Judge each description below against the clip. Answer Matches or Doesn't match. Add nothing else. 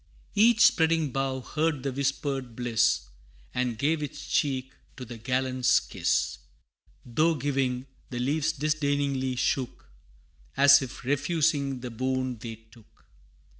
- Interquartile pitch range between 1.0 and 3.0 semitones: Matches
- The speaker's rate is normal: Doesn't match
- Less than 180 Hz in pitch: Matches